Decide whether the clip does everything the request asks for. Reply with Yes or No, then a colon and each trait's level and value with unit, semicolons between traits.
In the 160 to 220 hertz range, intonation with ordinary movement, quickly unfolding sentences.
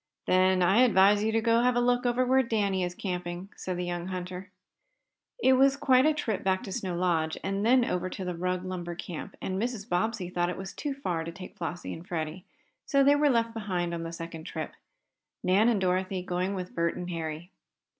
Yes: medium, 185 Hz; average, 4.4 semitones; fast, 210 wpm